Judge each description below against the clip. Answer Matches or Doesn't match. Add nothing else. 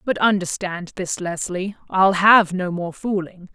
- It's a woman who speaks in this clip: Matches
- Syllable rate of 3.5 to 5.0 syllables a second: Matches